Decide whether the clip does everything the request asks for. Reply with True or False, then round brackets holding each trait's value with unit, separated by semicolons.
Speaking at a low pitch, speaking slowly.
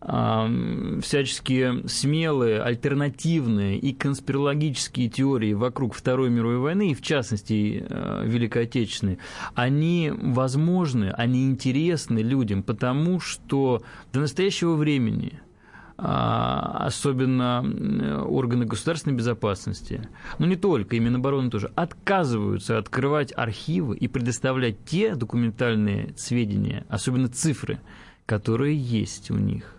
True (125 Hz; 105 wpm)